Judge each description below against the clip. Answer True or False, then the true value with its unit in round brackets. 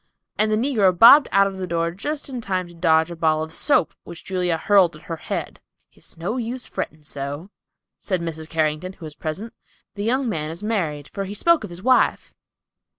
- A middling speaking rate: False (210 wpm)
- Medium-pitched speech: True (180 Hz)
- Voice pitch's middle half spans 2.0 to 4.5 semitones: False (4.9 semitones)